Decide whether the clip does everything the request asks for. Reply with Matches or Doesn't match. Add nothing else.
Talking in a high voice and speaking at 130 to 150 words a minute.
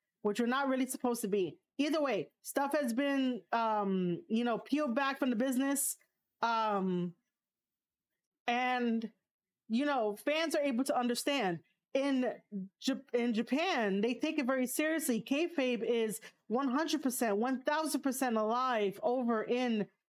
Matches